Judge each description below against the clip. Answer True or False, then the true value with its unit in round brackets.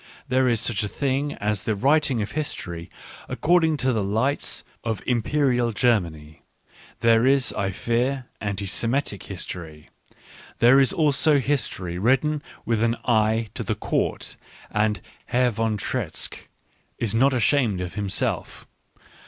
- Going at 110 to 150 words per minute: True (140 wpm)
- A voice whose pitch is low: True (115 Hz)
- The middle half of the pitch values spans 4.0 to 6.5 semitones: True (4.5 semitones)